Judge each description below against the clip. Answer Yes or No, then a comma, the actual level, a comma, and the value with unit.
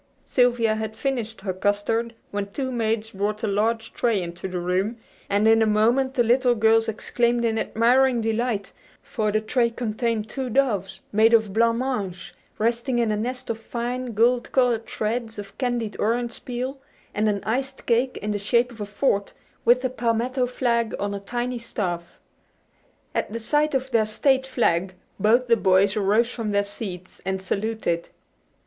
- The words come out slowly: No, average, 175 wpm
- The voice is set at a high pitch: Yes, high, 225 Hz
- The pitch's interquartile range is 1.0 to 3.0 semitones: Yes, average, 2.7 semitones